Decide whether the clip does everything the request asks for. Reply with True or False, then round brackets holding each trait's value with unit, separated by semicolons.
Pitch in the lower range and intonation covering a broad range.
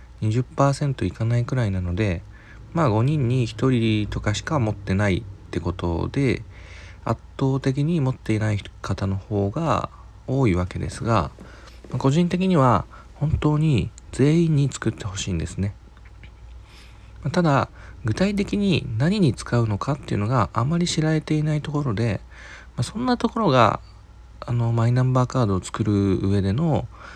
True (115 Hz; 6.0 semitones)